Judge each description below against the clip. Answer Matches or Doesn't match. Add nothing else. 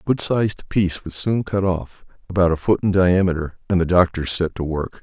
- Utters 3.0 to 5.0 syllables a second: Doesn't match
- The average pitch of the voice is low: Matches